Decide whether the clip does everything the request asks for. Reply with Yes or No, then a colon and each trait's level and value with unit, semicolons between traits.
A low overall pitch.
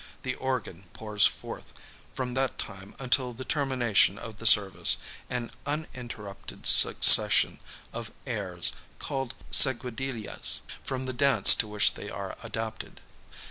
Yes: low, 120 Hz